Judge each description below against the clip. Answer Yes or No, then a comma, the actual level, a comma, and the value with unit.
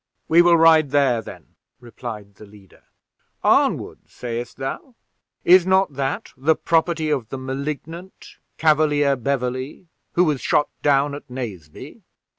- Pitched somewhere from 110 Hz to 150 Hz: Yes, medium, 140 Hz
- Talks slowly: Yes, slow, 130 wpm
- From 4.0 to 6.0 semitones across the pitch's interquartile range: Yes, average, 4.3 semitones